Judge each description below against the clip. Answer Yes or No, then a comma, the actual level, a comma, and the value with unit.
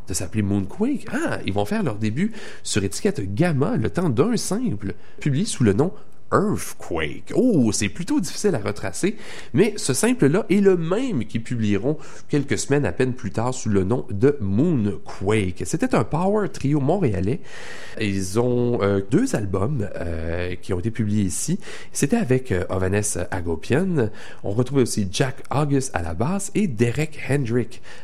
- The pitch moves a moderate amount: No, wide, 6.9 semitones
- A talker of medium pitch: No, low, 120 Hz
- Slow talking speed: No, average, 170 wpm